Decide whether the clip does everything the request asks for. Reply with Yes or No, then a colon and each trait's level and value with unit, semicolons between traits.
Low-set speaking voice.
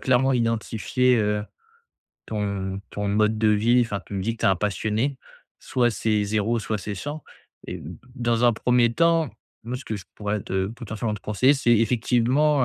Yes: low, 115 Hz